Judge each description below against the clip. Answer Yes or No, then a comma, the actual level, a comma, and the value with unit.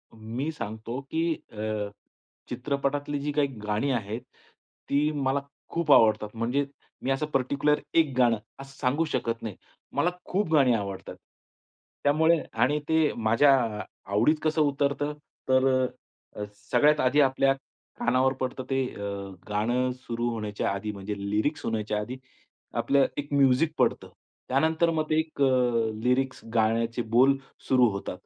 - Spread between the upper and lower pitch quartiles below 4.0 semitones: No, average, 4.5 semitones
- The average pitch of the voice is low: Yes, low, 130 Hz